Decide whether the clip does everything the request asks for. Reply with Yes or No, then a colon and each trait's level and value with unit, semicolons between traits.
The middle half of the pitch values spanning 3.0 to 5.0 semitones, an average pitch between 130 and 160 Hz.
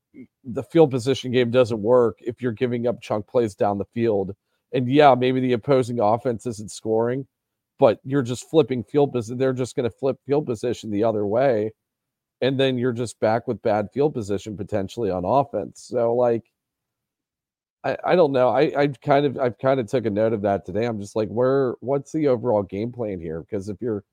No: average, 3.3 semitones; low, 120 Hz